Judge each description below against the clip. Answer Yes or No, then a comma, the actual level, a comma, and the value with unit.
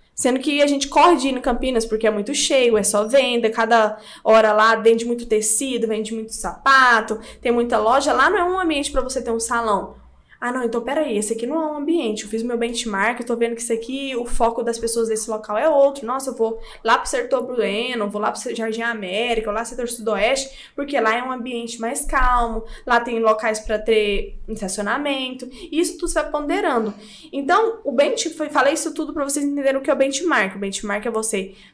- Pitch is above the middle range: Yes, high, 235 Hz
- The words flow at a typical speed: No, fast, 230 wpm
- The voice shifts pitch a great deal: No, average, 3.8 semitones